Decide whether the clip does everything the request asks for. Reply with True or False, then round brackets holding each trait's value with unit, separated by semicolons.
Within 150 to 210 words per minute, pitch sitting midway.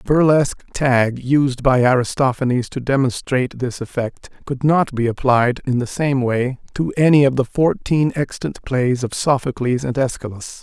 False (165 wpm; 130 Hz)